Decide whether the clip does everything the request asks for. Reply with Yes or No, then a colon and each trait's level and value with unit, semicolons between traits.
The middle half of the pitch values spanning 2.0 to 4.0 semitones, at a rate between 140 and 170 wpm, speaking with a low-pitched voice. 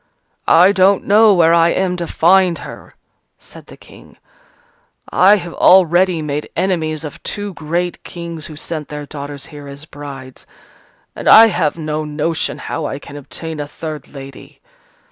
No: average, 3.3 semitones; average, 160 wpm; medium, 160 Hz